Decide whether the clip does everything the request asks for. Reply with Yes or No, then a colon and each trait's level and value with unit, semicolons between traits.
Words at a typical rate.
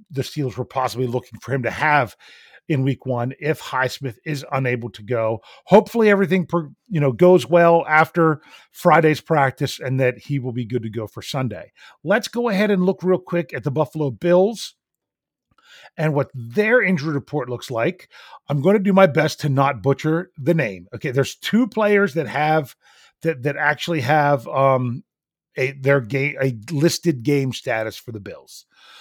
Yes: average, 180 wpm